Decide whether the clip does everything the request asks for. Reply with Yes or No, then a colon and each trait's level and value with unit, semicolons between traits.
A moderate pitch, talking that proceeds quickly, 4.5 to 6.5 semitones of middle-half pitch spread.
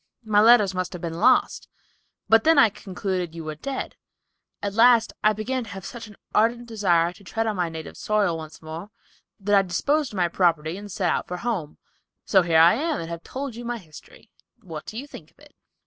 No: high, 200 Hz; fast, 215 wpm; average, 5.2 semitones